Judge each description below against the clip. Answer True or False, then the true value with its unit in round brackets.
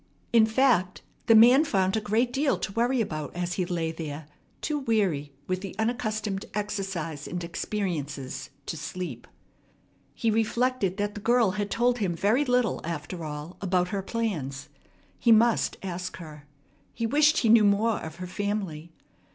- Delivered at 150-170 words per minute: True (160 wpm)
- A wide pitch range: False (5.0 semitones)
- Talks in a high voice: True (200 Hz)